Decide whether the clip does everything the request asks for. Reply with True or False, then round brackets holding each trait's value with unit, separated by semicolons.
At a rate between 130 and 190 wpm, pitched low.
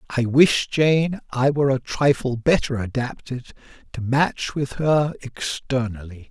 True (135 wpm; 130 Hz)